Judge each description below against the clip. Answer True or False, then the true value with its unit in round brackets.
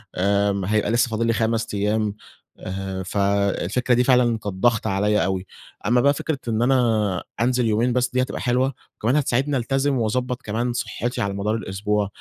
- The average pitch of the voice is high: False (110 Hz)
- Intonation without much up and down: False (3.5 semitones)